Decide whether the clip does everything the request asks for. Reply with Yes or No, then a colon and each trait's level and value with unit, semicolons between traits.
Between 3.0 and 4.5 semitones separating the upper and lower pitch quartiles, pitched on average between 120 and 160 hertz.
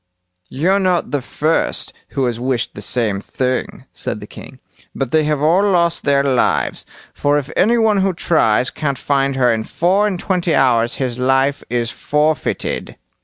No: average, 5.2 semitones; medium, 140 Hz